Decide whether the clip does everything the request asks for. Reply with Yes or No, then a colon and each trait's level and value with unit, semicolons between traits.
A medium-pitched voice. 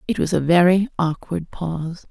Yes: medium, 170 Hz